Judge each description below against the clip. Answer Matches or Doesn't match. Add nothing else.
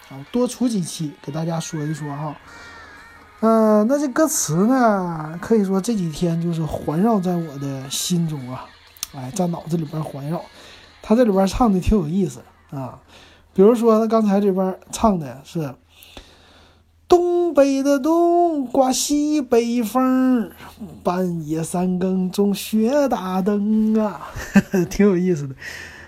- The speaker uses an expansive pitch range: Matches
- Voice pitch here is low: Doesn't match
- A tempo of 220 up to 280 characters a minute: Doesn't match